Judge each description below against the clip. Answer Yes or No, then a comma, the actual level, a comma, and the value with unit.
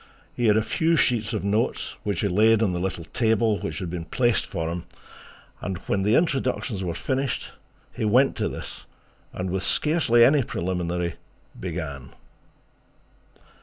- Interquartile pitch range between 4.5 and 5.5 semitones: Yes, average, 5.2 semitones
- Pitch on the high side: No, low, 105 Hz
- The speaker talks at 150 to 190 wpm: Yes, average, 160 wpm